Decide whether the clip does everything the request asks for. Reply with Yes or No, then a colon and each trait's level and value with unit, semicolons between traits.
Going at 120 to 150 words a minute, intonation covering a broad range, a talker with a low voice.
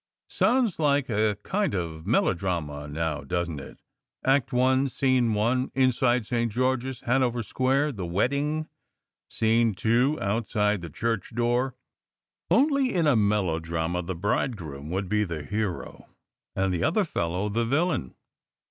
Yes: average, 145 wpm; wide, 6.5 semitones; low, 115 Hz